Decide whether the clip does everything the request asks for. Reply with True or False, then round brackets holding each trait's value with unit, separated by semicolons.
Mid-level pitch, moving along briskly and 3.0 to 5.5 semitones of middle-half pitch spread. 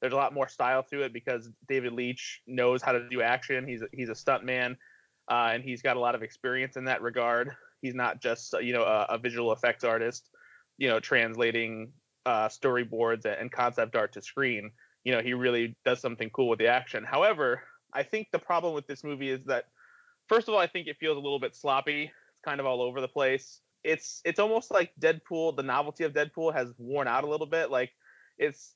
False (130 Hz; 220 wpm; 3.8 semitones)